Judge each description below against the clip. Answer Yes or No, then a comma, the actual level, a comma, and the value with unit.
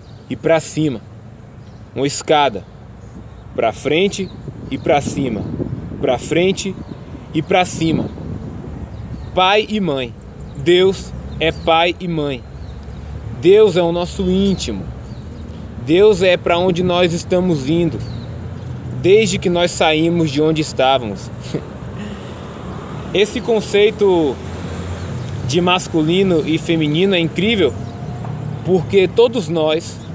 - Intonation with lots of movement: Yes, wide, 7.2 semitones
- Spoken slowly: Yes, slow, 105 wpm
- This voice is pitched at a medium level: Yes, medium, 160 Hz